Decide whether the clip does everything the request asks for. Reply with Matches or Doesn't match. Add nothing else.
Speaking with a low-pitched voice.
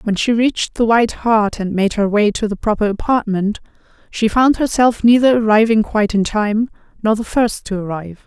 Doesn't match